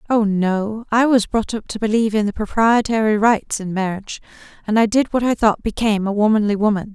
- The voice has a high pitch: Yes, high, 215 Hz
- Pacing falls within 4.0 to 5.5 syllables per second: No, 5.8 syllables/s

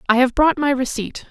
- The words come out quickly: Yes, fast, 230 wpm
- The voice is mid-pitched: No, very high, 265 Hz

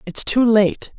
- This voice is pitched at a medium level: No, high, 225 Hz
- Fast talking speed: No, average, 185 wpm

